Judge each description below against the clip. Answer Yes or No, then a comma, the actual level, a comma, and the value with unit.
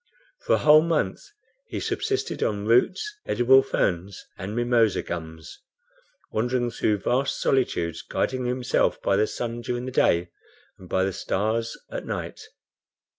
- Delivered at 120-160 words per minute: Yes, average, 140 wpm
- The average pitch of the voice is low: Yes, low, 120 Hz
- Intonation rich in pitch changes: No, average, 4.7 semitones